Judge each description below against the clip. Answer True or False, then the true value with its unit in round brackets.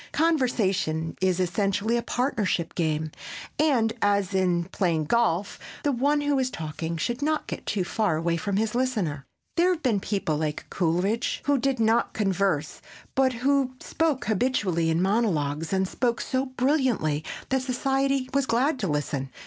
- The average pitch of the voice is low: False (210 Hz)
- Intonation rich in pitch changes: True (7.2 semitones)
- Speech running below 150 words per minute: False (155 wpm)